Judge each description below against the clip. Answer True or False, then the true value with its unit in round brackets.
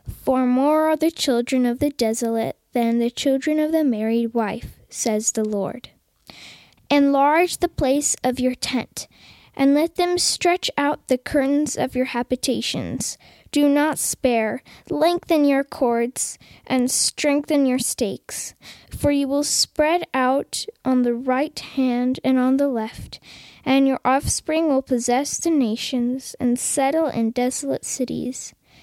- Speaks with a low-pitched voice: False (265 Hz)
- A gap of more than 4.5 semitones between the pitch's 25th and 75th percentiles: False (2.9 semitones)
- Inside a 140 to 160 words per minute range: True (145 wpm)